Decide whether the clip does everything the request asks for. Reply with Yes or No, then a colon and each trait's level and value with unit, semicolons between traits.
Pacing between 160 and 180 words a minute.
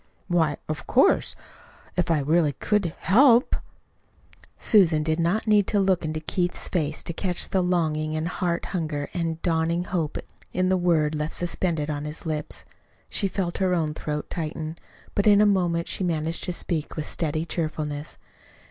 Yes: average, 170 wpm